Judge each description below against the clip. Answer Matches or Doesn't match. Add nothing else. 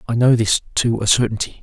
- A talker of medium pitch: Doesn't match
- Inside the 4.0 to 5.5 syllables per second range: Matches